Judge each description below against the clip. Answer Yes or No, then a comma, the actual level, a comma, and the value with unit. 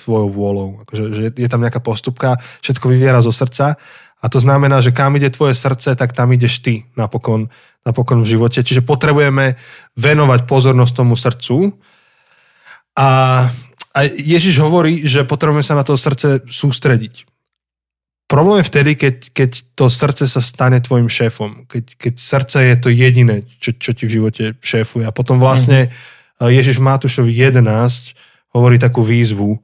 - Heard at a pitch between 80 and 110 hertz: No, low, 125 Hz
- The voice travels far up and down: No, narrow, 2.4 semitones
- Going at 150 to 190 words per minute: Yes, average, 155 wpm